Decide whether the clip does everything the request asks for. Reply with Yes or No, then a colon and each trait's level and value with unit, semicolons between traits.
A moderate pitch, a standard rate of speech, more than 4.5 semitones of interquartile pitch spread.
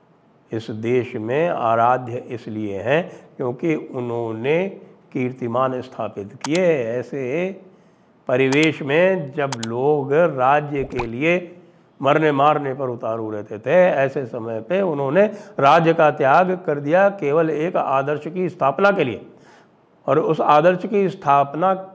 No: medium, 145 Hz; slow, 125 wpm; wide, 5.6 semitones